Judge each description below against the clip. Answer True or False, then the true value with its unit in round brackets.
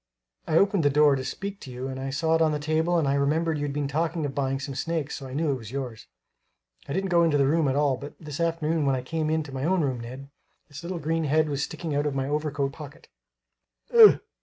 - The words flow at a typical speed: False (260 wpm)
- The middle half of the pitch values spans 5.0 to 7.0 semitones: False (2.9 semitones)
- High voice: False (145 Hz)